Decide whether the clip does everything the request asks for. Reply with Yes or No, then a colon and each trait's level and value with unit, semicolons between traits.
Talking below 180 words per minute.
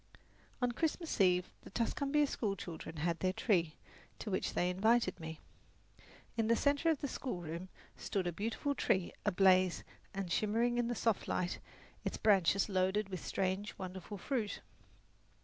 Yes: average, 150 wpm